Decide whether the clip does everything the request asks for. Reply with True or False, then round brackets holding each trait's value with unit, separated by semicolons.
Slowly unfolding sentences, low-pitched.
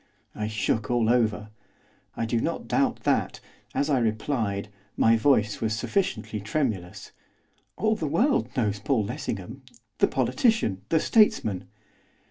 True (130 wpm; 115 Hz)